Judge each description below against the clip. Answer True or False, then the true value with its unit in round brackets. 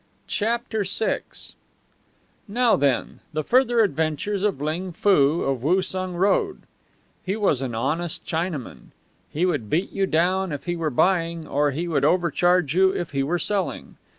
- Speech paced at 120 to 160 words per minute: True (150 wpm)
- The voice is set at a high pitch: False (175 Hz)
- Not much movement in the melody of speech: False (4.2 semitones)